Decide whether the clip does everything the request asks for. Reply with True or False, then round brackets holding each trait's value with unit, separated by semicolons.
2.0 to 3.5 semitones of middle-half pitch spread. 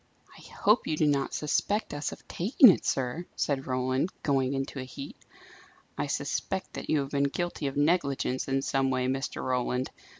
True (2.7 semitones)